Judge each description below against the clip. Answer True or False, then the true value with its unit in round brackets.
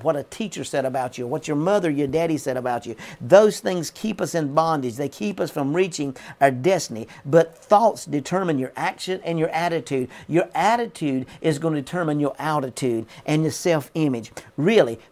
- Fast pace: False (190 wpm)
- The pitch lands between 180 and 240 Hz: False (155 Hz)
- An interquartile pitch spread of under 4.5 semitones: True (3.8 semitones)